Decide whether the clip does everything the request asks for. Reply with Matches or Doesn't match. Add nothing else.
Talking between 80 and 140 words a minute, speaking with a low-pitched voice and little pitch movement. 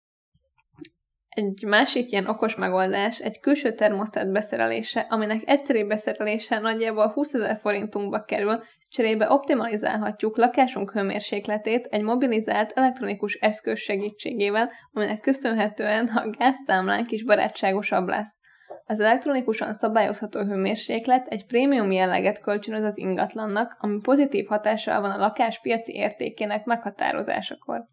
Doesn't match